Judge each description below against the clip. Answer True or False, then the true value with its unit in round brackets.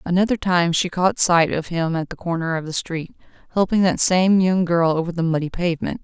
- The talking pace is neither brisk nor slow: False (220 wpm)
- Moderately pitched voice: True (175 Hz)